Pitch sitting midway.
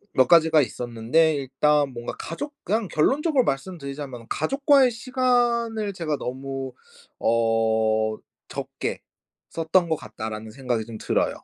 Yes: medium, 145 Hz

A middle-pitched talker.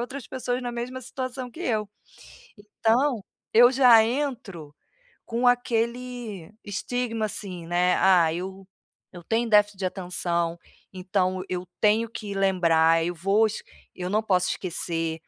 No: high, 210 Hz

